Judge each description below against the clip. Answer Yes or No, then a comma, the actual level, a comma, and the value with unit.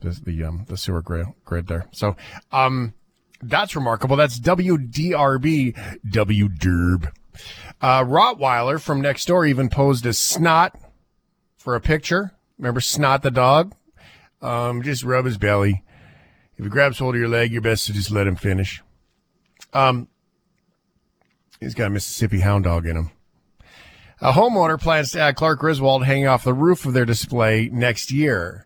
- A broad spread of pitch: Yes, wide, 6.3 semitones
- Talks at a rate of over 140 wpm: Yes, average, 155 wpm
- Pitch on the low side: Yes, low, 125 Hz